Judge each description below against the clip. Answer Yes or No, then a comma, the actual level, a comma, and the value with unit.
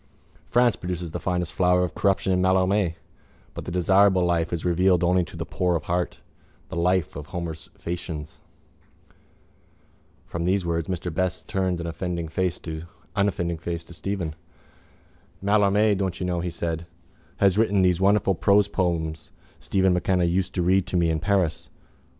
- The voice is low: Yes, very low, 90 Hz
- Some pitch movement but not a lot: No, narrow, 2.0 semitones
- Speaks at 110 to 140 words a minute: No, average, 155 wpm